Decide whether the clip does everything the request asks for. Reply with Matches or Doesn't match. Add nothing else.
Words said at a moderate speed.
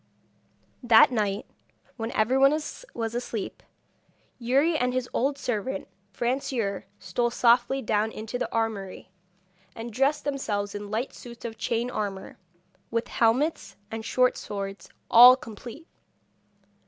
Doesn't match